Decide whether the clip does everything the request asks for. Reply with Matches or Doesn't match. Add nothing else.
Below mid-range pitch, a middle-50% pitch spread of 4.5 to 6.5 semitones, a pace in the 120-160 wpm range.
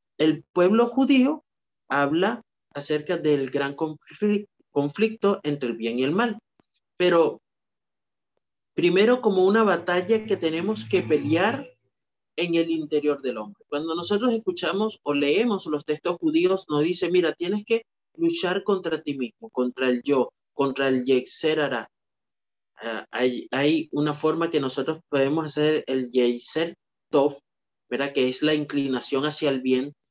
Doesn't match